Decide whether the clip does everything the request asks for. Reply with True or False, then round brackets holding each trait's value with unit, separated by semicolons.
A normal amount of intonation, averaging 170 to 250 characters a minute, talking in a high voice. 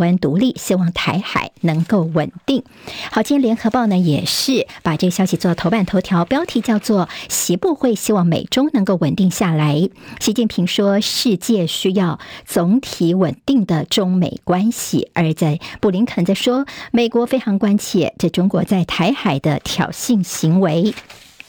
True (4.9 semitones; 245 characters per minute; 195 Hz)